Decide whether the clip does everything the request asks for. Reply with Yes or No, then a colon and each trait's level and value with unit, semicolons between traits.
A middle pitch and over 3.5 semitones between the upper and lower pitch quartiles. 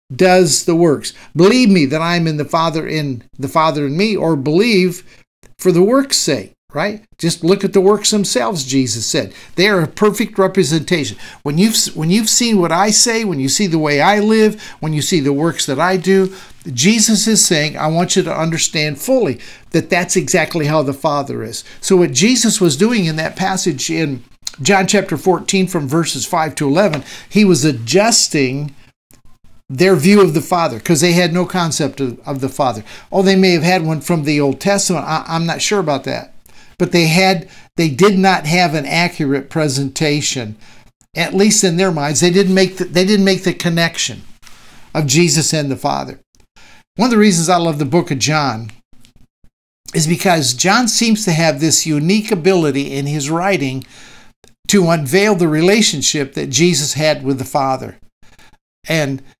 Yes: medium, 170 Hz; average, 4.7 semitones